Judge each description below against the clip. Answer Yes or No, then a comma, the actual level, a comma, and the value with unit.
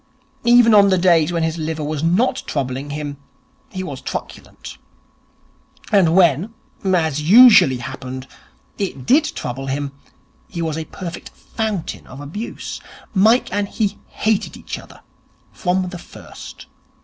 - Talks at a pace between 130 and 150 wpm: Yes, slow, 135 wpm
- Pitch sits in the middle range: Yes, medium, 170 Hz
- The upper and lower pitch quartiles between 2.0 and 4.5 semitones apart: No, wide, 5.4 semitones